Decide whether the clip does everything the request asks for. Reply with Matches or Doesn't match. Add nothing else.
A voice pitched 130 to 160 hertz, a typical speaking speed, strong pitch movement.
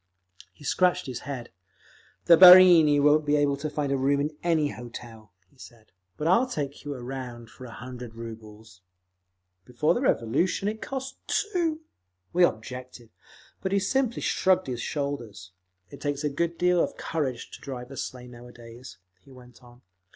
Matches